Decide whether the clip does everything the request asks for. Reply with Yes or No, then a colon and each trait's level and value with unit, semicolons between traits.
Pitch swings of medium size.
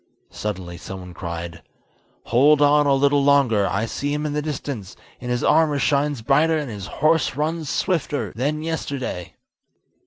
No: wide, 5.8 semitones